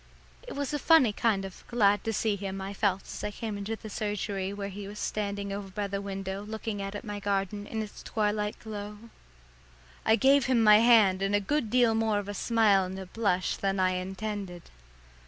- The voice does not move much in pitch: Yes, narrow, 2.0 semitones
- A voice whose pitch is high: Yes, high, 205 Hz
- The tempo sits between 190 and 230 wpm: Yes, fast, 205 wpm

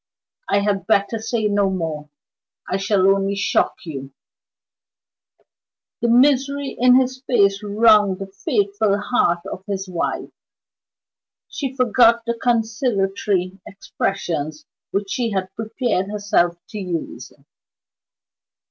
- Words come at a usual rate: No, slow, 110 wpm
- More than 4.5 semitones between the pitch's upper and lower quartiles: No, average, 3.4 semitones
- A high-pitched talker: Yes, high, 205 Hz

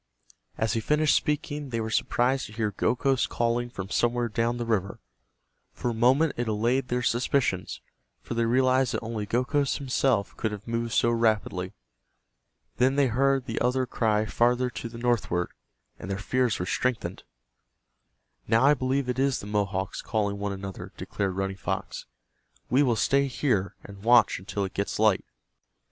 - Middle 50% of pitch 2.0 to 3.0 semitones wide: No, average, 3.6 semitones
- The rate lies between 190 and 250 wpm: No, average, 170 wpm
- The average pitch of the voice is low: Yes, low, 115 Hz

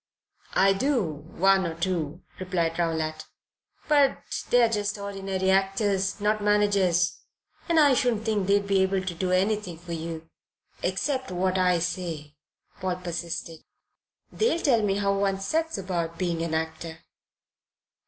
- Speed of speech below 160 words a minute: Yes, average, 140 wpm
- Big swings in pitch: No, average, 3.3 semitones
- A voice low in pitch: No, high, 190 Hz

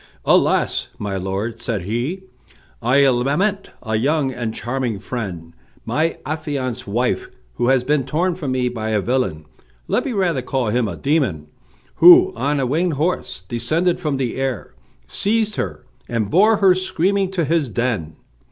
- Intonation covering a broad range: Yes, wide, 6.5 semitones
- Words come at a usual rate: Yes, average, 160 wpm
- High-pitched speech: No, low, 130 Hz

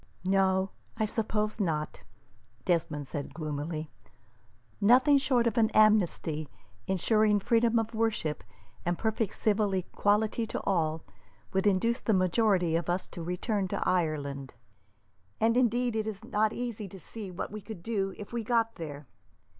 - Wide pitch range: No, average, 4.5 semitones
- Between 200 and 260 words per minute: No, average, 145 wpm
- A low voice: No, high, 200 Hz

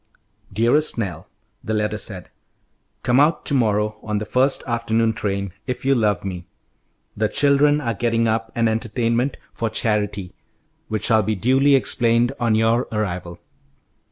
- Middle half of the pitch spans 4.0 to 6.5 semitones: No, narrow, 2.4 semitones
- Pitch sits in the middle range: No, low, 115 Hz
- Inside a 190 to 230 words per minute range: No, average, 150 wpm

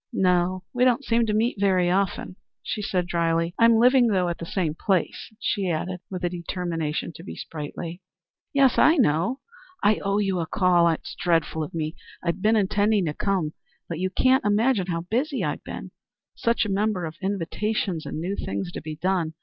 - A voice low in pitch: No, medium, 185 Hz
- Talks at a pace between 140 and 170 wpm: No, average, 190 wpm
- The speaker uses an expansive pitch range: No, average, 3.9 semitones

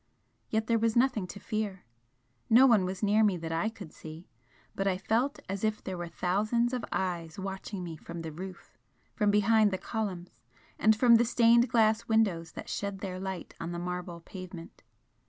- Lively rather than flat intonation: No, average, 3.7 semitones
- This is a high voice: Yes, high, 195 Hz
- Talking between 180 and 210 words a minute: Yes, average, 190 wpm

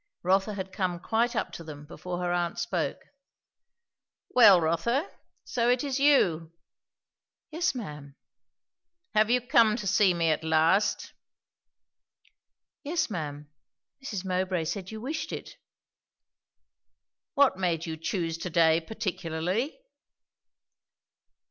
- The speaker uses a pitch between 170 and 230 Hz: Yes, medium, 185 Hz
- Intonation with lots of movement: Yes, wide, 6.0 semitones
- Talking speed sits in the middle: No, slow, 115 wpm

